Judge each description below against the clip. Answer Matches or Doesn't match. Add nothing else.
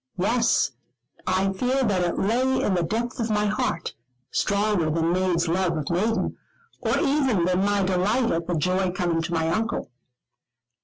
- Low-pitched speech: Doesn't match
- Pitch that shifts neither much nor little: Matches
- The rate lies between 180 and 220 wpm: Doesn't match